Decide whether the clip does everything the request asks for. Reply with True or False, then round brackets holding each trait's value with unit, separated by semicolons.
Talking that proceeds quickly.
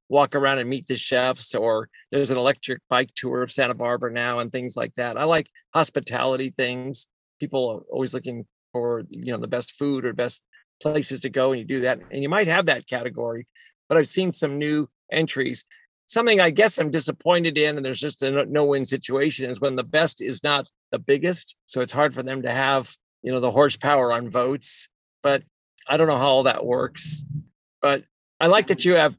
True (210 wpm)